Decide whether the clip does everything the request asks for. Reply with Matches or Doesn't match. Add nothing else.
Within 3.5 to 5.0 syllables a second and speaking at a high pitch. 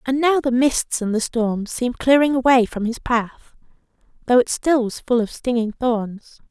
Matches